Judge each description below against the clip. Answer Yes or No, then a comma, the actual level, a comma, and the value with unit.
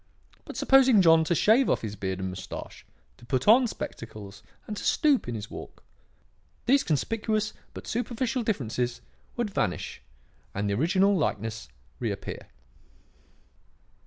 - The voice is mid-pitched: Yes, medium, 165 Hz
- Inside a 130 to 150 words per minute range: Yes, slow, 135 wpm